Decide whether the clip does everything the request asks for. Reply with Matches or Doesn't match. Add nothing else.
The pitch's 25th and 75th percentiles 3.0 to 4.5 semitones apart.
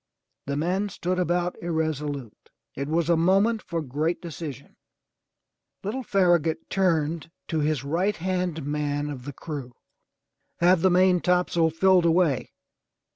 Matches